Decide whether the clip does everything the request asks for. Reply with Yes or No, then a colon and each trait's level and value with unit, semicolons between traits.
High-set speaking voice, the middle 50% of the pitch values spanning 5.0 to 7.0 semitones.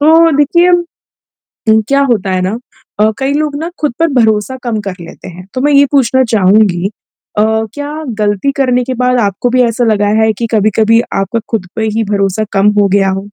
Yes: high, 225 Hz; wide, 5.5 semitones